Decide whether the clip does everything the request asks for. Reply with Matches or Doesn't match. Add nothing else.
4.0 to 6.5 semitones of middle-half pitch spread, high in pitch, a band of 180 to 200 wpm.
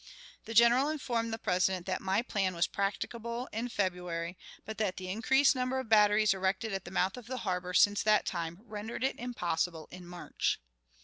Matches